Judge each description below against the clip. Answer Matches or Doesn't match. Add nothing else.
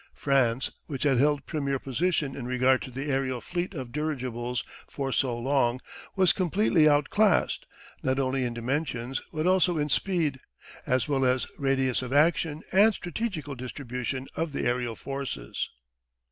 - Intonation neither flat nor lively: Matches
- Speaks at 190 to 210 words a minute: Doesn't match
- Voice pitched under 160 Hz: Matches